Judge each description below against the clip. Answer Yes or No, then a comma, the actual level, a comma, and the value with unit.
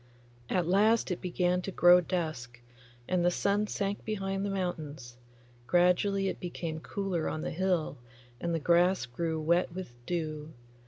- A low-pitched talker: No, medium, 175 Hz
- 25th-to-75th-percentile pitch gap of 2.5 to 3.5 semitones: Yes, average, 3.1 semitones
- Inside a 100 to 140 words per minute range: No, average, 155 wpm